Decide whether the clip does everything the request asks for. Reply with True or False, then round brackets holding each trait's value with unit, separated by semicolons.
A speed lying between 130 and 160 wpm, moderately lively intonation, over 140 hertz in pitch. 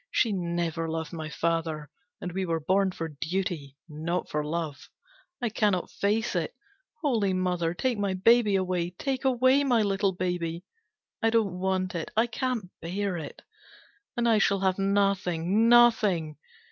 True (155 wpm; 4.2 semitones; 185 Hz)